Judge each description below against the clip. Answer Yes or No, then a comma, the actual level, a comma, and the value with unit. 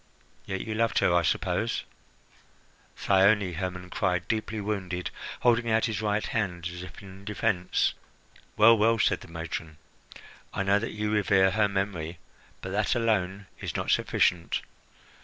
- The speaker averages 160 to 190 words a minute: No, average, 150 wpm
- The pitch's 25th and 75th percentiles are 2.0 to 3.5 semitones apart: Yes, average, 3.1 semitones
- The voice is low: Yes, low, 100 Hz